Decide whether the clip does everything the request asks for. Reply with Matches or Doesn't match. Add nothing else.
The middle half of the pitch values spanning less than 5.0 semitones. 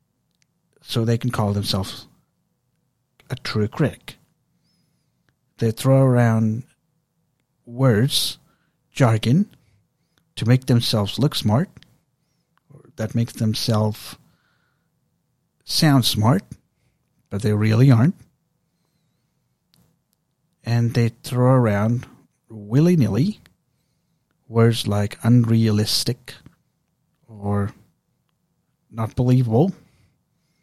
Doesn't match